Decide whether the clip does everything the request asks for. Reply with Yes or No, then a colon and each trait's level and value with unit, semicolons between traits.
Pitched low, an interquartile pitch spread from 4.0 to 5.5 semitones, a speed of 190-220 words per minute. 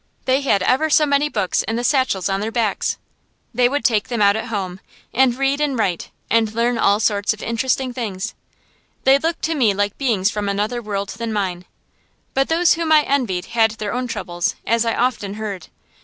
No: high, 230 Hz; average, 4.5 semitones; average, 200 wpm